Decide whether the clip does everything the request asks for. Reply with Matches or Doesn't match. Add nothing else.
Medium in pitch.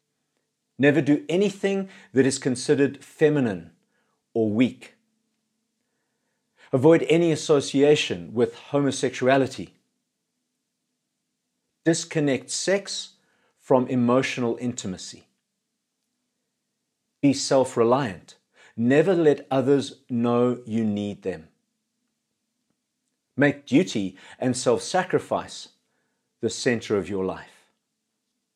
Matches